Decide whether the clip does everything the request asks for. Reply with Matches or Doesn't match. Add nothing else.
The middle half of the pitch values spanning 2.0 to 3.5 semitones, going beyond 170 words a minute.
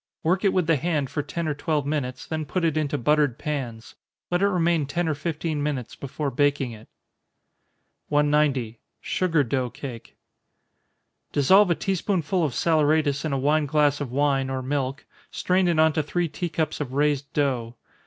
Matches